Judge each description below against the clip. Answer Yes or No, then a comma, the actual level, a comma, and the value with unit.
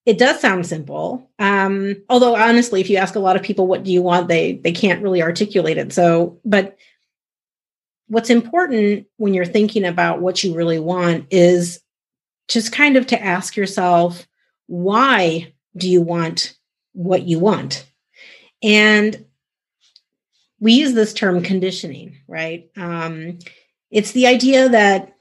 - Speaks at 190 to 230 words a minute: No, average, 150 wpm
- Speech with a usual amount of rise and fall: Yes, average, 3.7 semitones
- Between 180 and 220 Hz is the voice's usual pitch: Yes, high, 190 Hz